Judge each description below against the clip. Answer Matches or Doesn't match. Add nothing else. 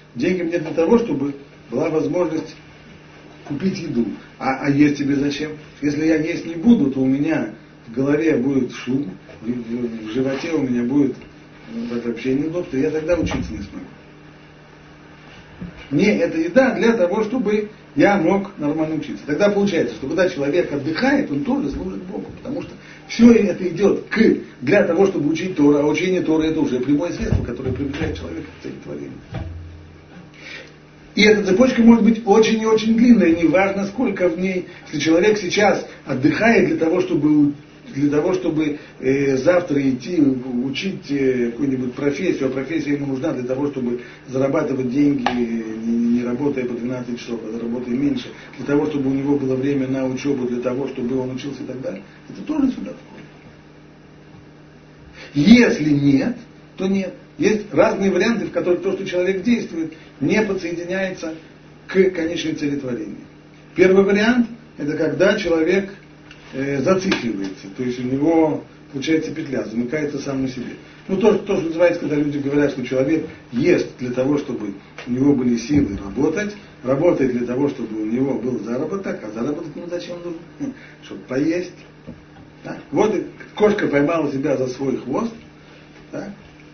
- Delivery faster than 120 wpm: Matches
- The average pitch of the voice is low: Doesn't match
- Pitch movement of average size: Doesn't match